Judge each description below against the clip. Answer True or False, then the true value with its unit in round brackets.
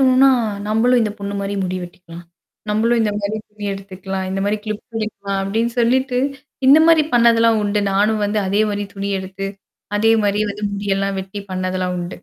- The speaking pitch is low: False (205 Hz)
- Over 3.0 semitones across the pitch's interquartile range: False (2.5 semitones)